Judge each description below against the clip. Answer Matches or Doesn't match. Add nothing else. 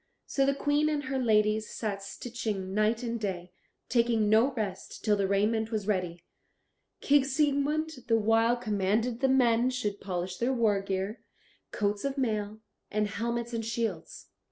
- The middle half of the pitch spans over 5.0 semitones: Doesn't match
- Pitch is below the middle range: Doesn't match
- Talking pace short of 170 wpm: Matches